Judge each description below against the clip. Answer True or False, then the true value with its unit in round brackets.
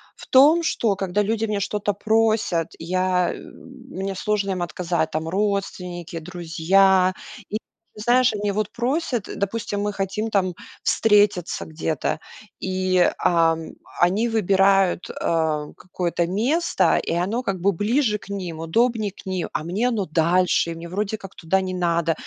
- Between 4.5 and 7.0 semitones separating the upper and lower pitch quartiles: False (3.3 semitones)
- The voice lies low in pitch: False (195 Hz)